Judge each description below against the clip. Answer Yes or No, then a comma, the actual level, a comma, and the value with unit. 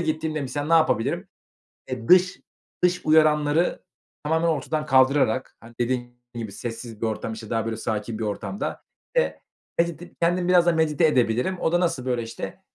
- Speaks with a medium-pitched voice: Yes, medium, 145 Hz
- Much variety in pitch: Yes, wide, 5.9 semitones